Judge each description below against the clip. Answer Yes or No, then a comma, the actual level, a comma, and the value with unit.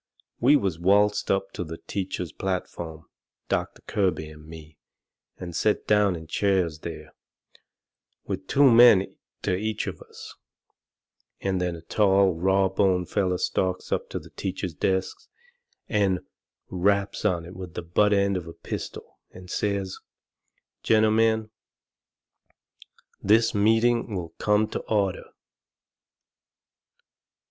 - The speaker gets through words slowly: Yes, slow, 125 wpm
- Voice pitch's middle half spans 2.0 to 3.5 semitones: Yes, narrow, 2.6 semitones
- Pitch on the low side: Yes, very low, 95 Hz